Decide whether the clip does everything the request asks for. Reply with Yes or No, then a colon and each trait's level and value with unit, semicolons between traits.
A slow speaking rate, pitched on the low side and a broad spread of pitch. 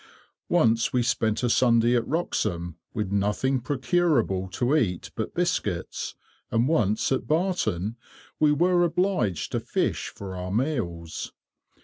Yes: slow, 130 wpm; low, 120 Hz; wide, 7.0 semitones